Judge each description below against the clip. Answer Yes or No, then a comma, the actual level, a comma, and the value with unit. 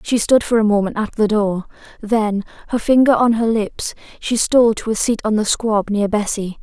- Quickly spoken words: Yes, fast, 210 wpm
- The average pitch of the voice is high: Yes, high, 220 Hz